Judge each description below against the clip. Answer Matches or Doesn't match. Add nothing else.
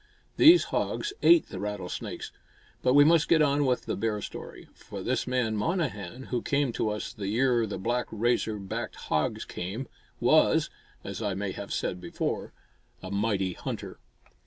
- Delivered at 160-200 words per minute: Matches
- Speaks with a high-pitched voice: Doesn't match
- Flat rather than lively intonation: Doesn't match